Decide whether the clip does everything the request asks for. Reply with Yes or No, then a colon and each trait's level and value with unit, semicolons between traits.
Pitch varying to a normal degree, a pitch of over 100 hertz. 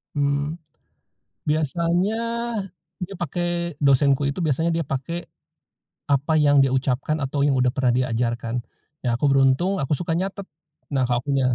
Yes: average, 3.8 semitones; medium, 140 Hz